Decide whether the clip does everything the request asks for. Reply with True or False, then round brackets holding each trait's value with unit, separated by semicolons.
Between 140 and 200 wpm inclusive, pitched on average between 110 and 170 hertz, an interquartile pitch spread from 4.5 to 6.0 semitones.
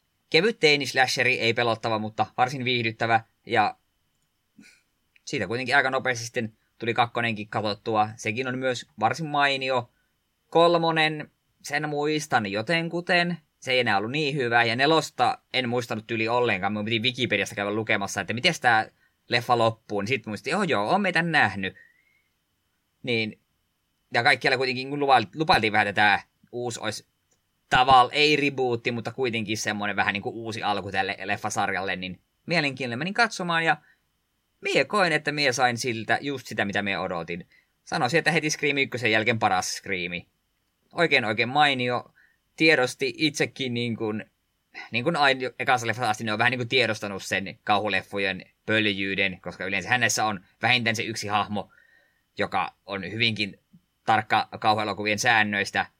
True (145 wpm; 120 Hz; 4.8 semitones)